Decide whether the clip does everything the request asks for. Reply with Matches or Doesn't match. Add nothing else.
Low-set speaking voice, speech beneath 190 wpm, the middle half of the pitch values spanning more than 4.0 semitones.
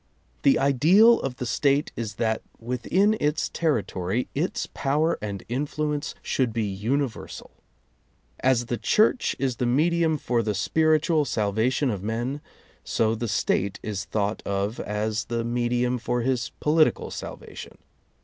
Matches